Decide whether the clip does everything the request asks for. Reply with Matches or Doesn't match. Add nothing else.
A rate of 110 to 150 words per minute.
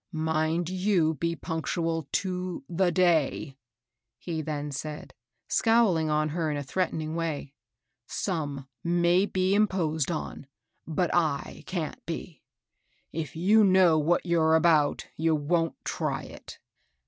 Matches